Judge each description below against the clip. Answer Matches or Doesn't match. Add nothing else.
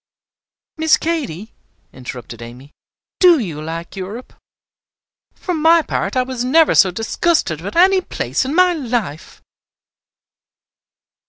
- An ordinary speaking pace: Doesn't match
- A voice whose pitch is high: Matches